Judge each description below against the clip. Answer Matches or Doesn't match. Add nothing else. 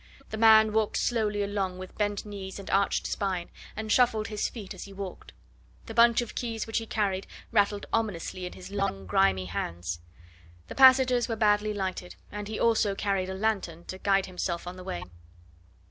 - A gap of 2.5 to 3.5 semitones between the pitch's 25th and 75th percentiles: Matches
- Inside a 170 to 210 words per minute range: Matches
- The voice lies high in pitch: Matches